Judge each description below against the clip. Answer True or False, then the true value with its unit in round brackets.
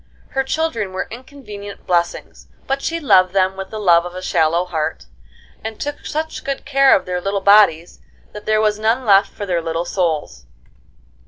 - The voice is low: False (200 Hz)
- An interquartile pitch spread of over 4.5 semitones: True (5.1 semitones)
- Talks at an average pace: True (180 wpm)